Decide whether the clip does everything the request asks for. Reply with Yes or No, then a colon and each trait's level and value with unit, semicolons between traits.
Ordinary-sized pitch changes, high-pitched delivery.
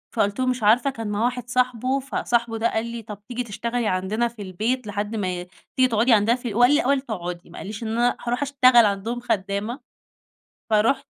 Yes: average, 3.1 semitones; high, 230 Hz